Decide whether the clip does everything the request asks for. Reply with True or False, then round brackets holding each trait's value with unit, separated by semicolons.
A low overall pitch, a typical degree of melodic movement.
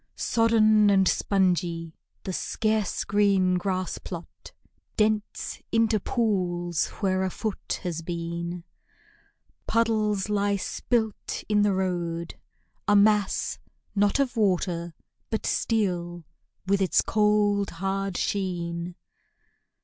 False (195 Hz; 3.2 semitones)